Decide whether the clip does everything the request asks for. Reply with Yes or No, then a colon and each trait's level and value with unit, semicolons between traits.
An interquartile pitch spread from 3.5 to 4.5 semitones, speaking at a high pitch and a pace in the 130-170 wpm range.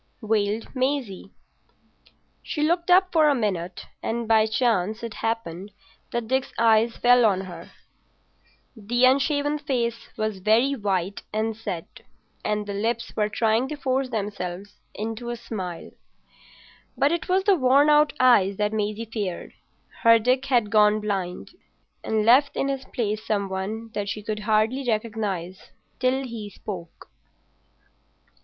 Yes: average, 3.8 semitones; high, 220 Hz; average, 145 wpm